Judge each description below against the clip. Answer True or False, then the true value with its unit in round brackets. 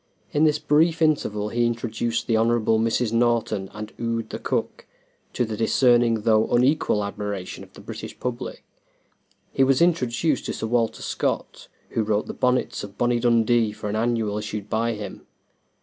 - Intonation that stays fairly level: True (2.1 semitones)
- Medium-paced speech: True (165 wpm)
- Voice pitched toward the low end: True (115 Hz)